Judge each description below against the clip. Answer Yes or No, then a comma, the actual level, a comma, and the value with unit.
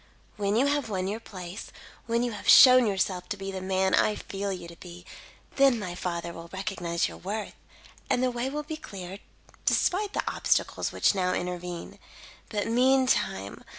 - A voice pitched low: No, high, 195 Hz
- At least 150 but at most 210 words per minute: Yes, average, 180 wpm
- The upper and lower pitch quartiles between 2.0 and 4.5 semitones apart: No, average, 5.0 semitones